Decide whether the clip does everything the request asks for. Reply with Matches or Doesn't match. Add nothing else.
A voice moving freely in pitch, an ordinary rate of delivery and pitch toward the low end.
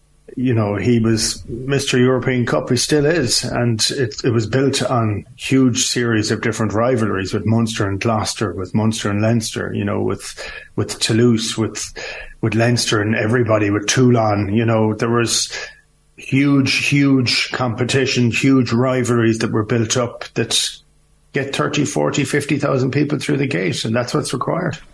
Doesn't match